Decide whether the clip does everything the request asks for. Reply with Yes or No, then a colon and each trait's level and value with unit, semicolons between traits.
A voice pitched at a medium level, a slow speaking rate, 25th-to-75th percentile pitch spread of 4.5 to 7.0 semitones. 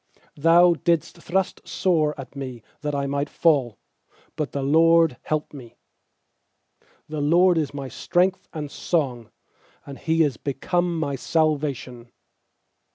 No: medium, 150 Hz; slow, 130 wpm; average, 3.1 semitones